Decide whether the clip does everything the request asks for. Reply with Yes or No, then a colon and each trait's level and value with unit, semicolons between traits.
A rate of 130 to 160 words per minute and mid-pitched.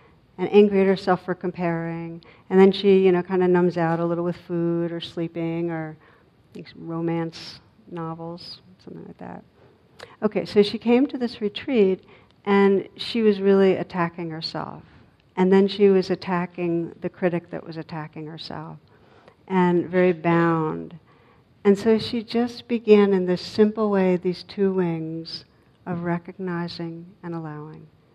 Yes: average, 150 wpm; medium, 180 Hz